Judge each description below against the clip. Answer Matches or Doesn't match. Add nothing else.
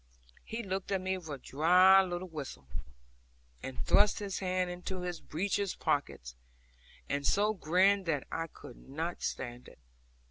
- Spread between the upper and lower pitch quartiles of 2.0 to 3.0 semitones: Doesn't match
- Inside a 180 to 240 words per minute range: Doesn't match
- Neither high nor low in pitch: Matches